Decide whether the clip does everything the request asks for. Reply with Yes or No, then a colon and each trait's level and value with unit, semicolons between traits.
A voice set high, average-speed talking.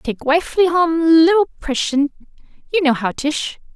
No: very high, 310 Hz; slow, 130 wpm